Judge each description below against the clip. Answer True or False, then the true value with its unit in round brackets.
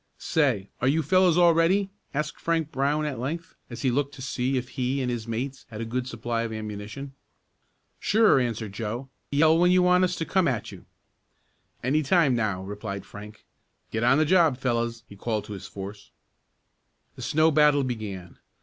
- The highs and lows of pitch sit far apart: True (5.7 semitones)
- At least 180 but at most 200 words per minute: True (185 wpm)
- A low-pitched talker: True (130 Hz)